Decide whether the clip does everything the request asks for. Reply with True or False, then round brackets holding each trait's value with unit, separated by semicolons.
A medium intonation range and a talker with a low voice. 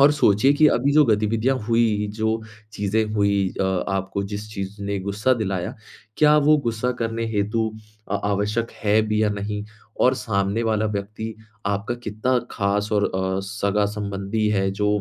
False (2.0 semitones; 105 Hz)